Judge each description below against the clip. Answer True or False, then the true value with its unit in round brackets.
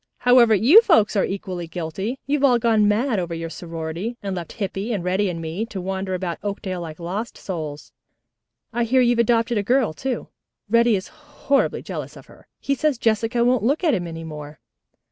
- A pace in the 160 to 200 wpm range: True (195 wpm)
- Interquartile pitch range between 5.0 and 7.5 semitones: True (5.4 semitones)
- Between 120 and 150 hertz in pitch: False (205 Hz)